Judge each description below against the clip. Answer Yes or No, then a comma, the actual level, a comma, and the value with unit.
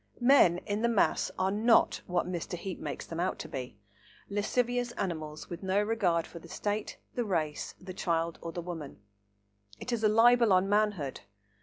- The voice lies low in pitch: No, medium, 185 Hz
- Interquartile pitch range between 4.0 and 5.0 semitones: Yes, average, 4.3 semitones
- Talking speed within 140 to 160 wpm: No, average, 175 wpm